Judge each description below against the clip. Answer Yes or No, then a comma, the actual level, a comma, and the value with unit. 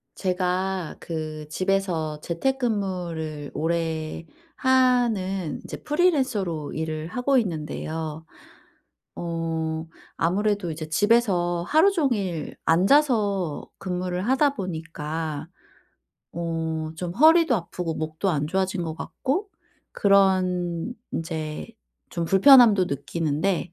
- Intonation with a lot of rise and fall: No, average, 4.3 semitones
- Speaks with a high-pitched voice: No, medium, 180 Hz